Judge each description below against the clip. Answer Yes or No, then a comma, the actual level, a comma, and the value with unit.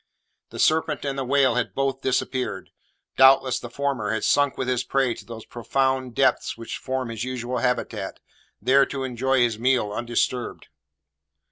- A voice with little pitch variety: Yes, narrow, 2.0 semitones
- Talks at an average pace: Yes, average, 160 wpm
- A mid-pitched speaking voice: No, low, 130 Hz